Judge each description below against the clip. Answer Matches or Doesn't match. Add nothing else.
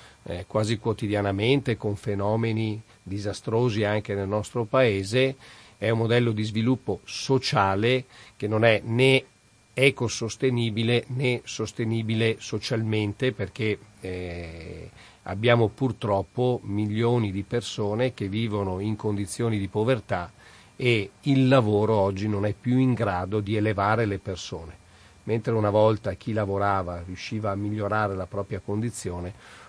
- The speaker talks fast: Doesn't match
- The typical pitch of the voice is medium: Doesn't match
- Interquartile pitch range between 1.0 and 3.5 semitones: Matches